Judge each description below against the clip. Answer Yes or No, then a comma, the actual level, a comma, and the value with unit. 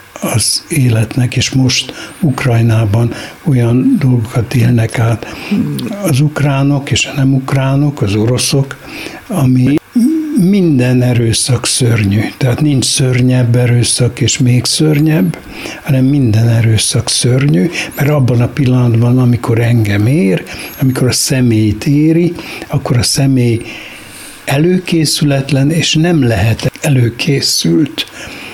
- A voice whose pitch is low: Yes, low, 130 Hz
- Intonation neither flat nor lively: Yes, average, 3.9 semitones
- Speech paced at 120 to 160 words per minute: No, slow, 105 wpm